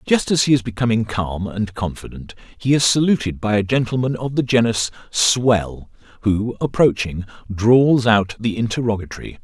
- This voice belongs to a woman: No, male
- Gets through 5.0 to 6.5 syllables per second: No, 4.8 syllables/s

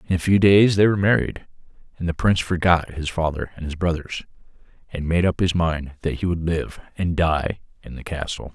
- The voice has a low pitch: Yes, very low, 85 Hz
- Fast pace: Yes, fast, 210 wpm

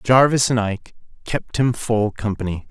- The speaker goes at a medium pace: Yes, average, 155 wpm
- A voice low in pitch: Yes, low, 115 Hz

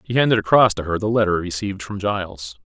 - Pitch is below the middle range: Yes, low, 100 Hz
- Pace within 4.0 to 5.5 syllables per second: No, 6.6 syllables/s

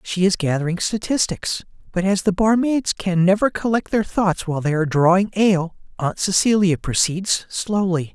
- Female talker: No, male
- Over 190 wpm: No, average, 160 wpm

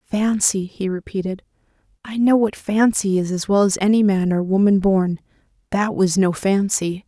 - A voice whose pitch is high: Yes, high, 200 Hz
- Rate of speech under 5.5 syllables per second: Yes, 4.6 syllables/s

